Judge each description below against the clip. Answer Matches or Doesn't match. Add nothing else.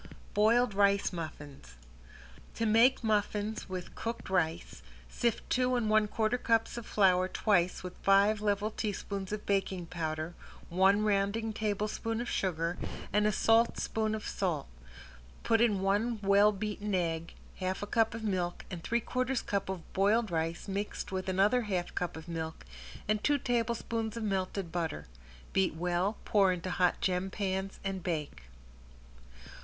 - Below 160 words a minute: Matches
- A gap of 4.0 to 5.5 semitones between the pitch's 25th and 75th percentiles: Doesn't match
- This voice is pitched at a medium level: Doesn't match